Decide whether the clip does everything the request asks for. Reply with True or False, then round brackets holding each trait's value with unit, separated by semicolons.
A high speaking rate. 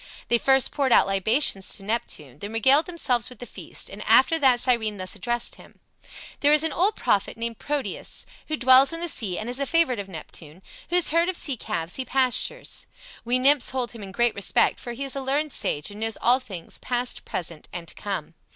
True (215 wpm)